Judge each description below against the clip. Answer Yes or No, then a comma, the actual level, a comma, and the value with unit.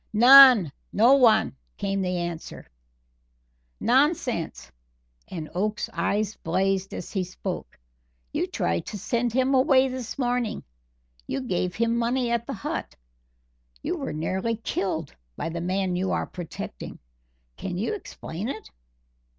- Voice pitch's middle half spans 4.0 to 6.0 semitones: Yes, average, 5.3 semitones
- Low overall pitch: No, high, 205 Hz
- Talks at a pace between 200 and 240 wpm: No, slow, 135 wpm